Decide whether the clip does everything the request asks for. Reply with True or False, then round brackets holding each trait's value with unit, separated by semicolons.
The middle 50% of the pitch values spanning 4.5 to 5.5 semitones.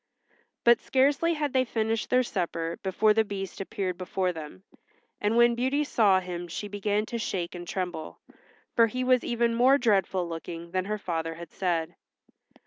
True (5.2 semitones)